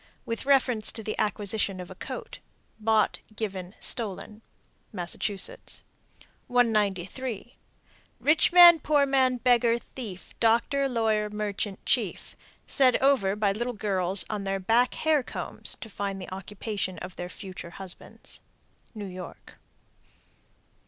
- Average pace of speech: No, slow, 125 wpm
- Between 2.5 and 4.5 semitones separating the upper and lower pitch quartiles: Yes, average, 4.1 semitones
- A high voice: Yes, high, 215 Hz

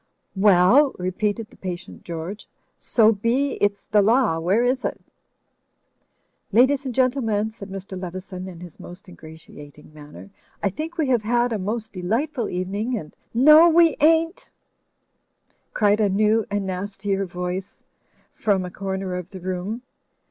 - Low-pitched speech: No, high, 205 Hz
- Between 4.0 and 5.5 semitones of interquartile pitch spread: Yes, average, 4.7 semitones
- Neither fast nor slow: Yes, average, 150 wpm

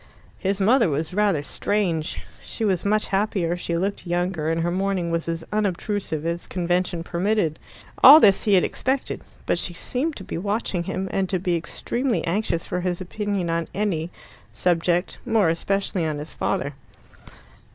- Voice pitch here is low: No, medium, 180 Hz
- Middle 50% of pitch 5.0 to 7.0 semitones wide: No, average, 3.4 semitones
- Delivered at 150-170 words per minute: Yes, average, 165 wpm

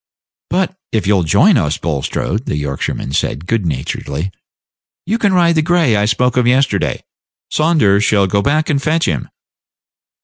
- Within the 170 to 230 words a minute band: No, average, 160 wpm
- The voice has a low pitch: Yes, low, 110 Hz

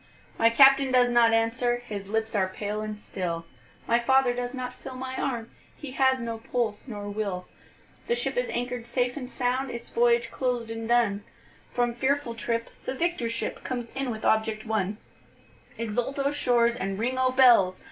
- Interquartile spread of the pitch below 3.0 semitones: Yes, narrow, 2.6 semitones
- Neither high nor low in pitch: No, high, 240 Hz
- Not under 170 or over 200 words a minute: Yes, average, 180 wpm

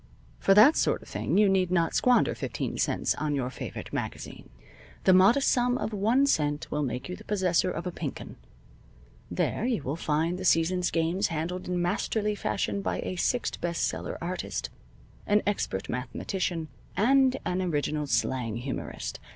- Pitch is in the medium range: Yes, medium, 180 Hz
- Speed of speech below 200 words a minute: Yes, average, 170 wpm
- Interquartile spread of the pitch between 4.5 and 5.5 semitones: Yes, average, 5.1 semitones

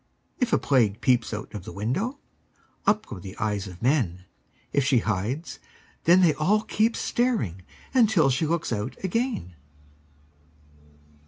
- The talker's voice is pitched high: No, low, 135 Hz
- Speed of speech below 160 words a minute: Yes, average, 145 wpm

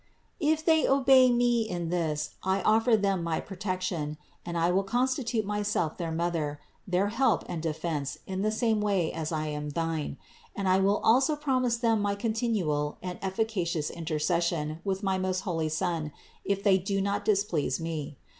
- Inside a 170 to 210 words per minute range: Yes, average, 175 wpm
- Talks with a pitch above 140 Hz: Yes, high, 190 Hz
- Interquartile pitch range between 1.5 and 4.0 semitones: No, average, 4.9 semitones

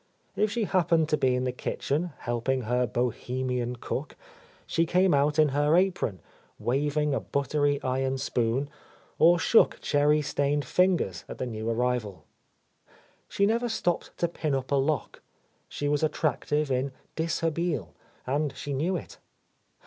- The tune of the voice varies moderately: Yes, average, 4.3 semitones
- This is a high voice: No, medium, 145 Hz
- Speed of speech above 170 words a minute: No, average, 150 wpm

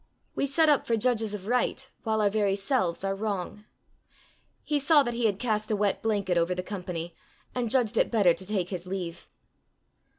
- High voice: Yes, high, 210 Hz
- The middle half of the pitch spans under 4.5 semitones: Yes, average, 4.1 semitones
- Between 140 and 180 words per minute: No, average, 195 wpm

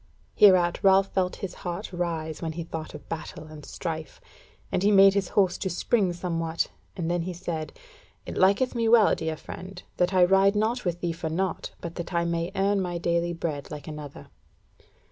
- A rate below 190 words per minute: No, average, 195 wpm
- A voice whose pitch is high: No, medium, 175 Hz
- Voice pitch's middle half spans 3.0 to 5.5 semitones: No, narrow, 2.6 semitones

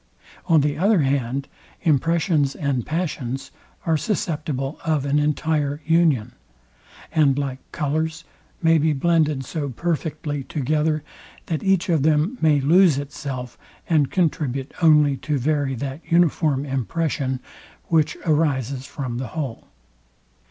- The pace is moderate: No, slow, 125 wpm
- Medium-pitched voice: Yes, medium, 150 Hz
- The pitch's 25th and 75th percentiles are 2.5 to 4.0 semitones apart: Yes, average, 2.9 semitones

